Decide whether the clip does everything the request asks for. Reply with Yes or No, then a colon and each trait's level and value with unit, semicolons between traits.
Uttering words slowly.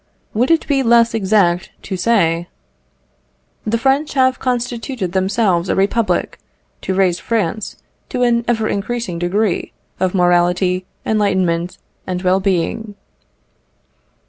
Yes: slow, 120 wpm